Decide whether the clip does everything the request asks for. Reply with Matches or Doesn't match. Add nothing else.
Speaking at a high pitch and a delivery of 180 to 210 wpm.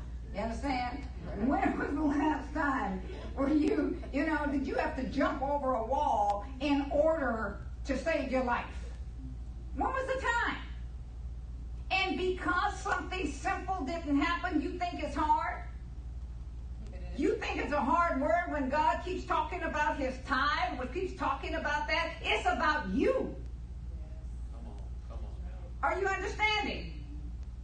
Doesn't match